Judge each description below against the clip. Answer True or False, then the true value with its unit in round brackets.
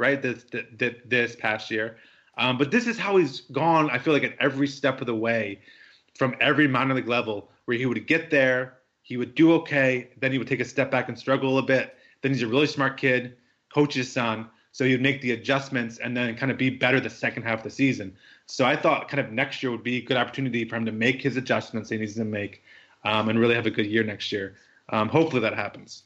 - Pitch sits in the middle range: False (125 Hz)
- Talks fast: True (255 wpm)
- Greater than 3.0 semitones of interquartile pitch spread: False (2.7 semitones)